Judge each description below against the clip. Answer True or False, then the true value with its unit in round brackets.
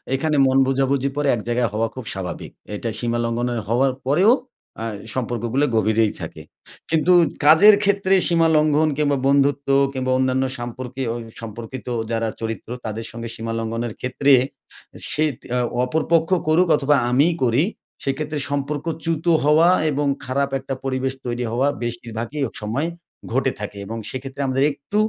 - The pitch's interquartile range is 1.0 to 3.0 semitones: False (3.9 semitones)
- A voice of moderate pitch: False (130 Hz)